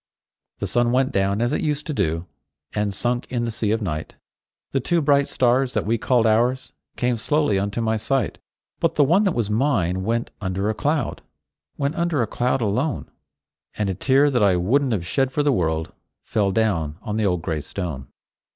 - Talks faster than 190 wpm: Yes, average, 200 wpm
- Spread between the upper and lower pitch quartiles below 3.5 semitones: No, wide, 5.4 semitones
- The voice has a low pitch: Yes, low, 115 Hz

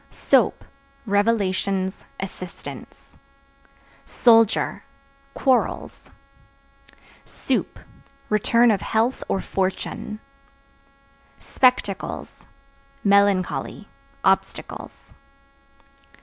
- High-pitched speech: Yes, high, 205 Hz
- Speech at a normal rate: No, slow, 50 wpm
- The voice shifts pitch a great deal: No, average, 2.9 semitones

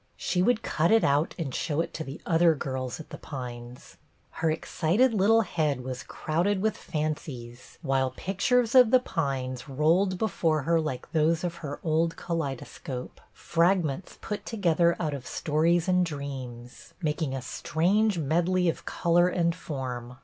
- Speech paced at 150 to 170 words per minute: Yes, average, 165 wpm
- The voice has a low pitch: No, medium, 160 Hz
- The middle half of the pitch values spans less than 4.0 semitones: No, average, 4.7 semitones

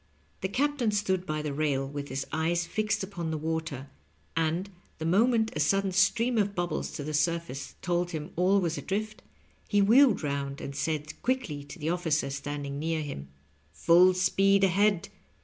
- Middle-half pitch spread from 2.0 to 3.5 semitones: No, average, 4.8 semitones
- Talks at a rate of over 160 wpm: Yes, average, 170 wpm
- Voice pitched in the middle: Yes, medium, 170 Hz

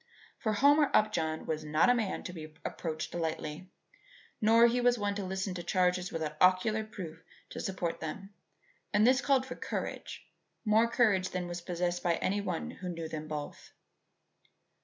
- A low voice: No, medium, 185 Hz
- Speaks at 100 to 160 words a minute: No, average, 170 wpm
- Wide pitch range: No, average, 4.5 semitones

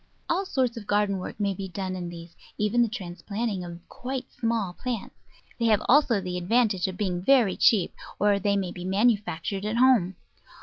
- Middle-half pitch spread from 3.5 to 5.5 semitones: Yes, average, 4.1 semitones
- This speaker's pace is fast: No, average, 185 wpm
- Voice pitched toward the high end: Yes, high, 205 Hz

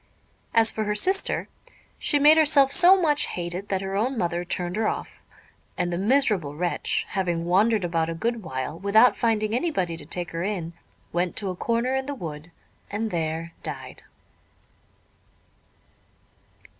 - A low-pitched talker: No, high, 195 Hz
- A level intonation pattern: No, wide, 5.4 semitones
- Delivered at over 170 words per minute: No, average, 155 wpm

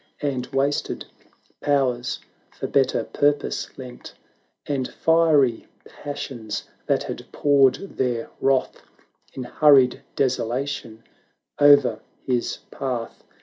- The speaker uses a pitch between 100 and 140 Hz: Yes, low, 135 Hz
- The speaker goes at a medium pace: No, slow, 95 wpm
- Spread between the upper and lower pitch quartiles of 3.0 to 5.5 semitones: No, narrow, 2.6 semitones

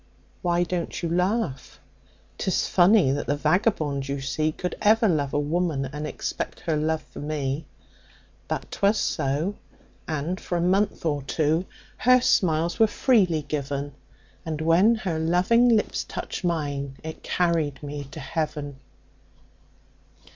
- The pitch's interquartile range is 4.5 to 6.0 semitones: No, average, 3.8 semitones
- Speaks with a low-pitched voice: No, medium, 160 Hz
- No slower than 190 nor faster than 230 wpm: No, average, 140 wpm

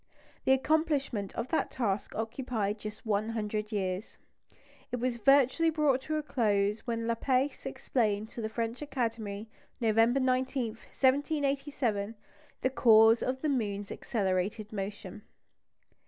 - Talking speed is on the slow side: Yes, slow, 125 wpm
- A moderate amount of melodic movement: Yes, average, 3.9 semitones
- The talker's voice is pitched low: No, high, 230 Hz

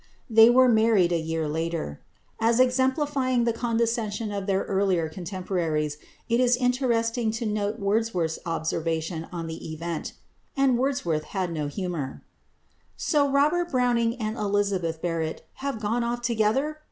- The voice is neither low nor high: No, high, 215 Hz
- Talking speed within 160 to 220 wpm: No, average, 140 wpm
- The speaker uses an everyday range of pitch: No, wide, 6.3 semitones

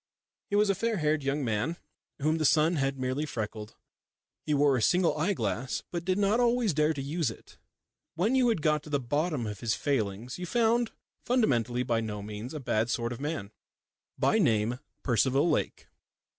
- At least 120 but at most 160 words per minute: No, average, 190 wpm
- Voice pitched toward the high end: No, medium, 145 Hz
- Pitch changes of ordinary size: No, wide, 6.7 semitones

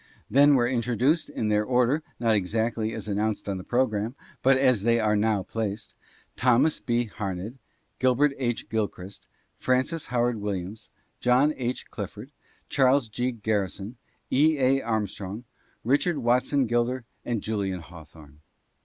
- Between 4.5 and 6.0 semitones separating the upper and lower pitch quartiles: No, average, 3.6 semitones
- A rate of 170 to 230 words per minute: No, average, 145 wpm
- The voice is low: Yes, low, 115 Hz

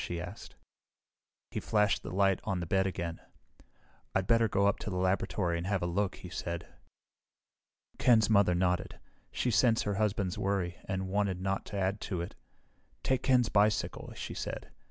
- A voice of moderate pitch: No, very low, 95 Hz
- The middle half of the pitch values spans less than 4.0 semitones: Yes, narrow, 2.6 semitones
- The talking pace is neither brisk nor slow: Yes, average, 175 wpm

